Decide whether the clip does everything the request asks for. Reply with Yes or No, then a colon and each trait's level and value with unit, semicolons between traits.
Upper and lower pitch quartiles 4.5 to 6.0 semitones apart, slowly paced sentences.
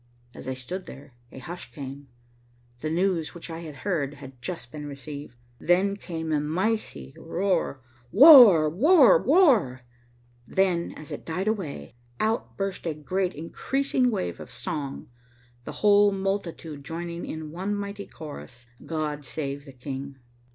No: wide, 5.6 semitones; average, 145 wpm